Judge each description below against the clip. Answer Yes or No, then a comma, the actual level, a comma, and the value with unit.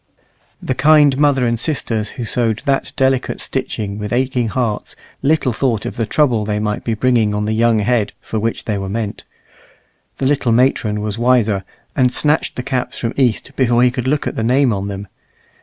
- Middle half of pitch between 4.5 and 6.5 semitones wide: No, average, 3.4 semitones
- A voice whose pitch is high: No, low, 120 Hz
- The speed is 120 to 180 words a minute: No, average, 195 wpm